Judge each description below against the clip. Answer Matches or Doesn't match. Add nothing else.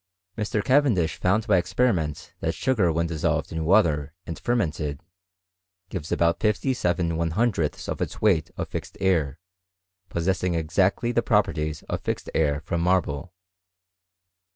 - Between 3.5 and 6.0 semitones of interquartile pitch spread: Matches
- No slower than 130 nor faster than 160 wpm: Matches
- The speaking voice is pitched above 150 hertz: Doesn't match